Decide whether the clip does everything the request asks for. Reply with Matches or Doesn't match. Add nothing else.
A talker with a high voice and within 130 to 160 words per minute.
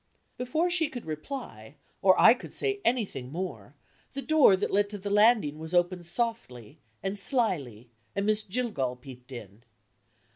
Matches